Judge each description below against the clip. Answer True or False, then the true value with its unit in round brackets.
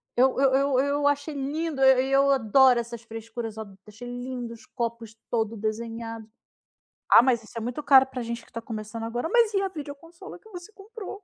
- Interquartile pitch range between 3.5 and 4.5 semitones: True (3.8 semitones)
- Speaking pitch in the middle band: False (250 Hz)